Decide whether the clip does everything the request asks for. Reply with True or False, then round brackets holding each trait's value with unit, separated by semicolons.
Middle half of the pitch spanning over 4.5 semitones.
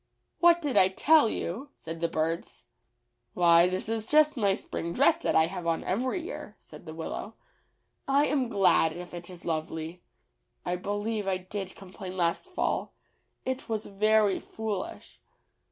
True (5.1 semitones)